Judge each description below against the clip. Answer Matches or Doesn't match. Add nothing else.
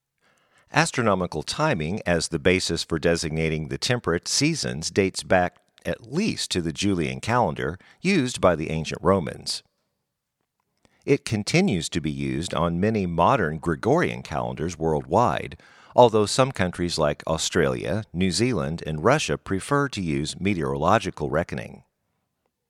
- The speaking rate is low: Matches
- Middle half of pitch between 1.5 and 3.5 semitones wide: Doesn't match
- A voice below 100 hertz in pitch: Matches